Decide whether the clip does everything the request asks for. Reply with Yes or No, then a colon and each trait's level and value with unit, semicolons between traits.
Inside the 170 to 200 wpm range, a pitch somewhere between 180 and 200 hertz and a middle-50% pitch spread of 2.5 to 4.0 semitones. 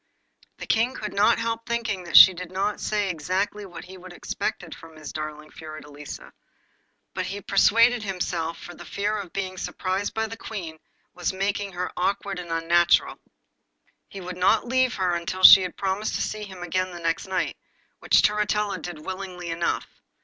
Yes: average, 180 wpm; medium, 185 Hz; average, 3.1 semitones